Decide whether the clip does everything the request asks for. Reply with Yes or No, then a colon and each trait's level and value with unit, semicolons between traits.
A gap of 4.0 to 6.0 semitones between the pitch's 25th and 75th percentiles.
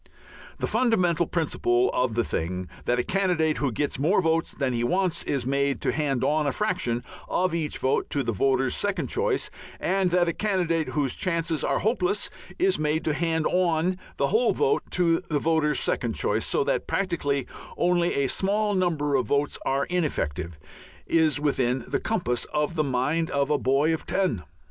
Yes: average, 4.7 semitones